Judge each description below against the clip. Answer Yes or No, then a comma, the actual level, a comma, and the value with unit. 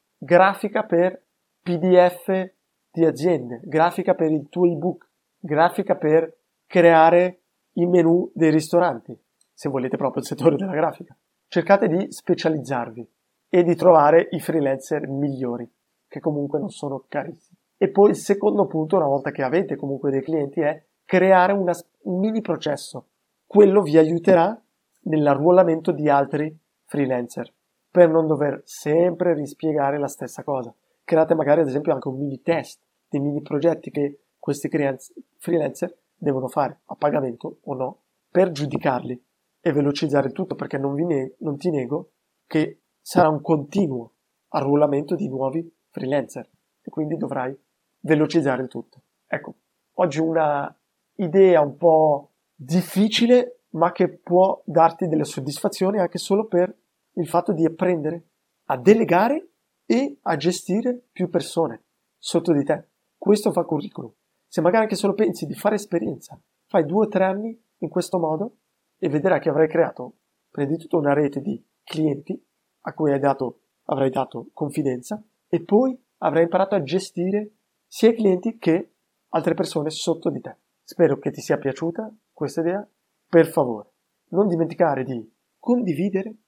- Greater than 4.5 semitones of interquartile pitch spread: No, average, 4.0 semitones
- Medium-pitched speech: Yes, medium, 165 Hz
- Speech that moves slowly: No, average, 145 wpm